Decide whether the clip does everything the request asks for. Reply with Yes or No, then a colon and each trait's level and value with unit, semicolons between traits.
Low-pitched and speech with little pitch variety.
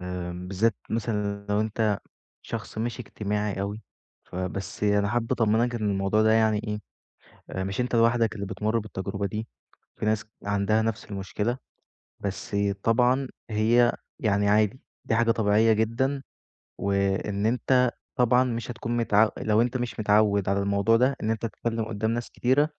Yes: low, 110 Hz; narrow, 2.3 semitones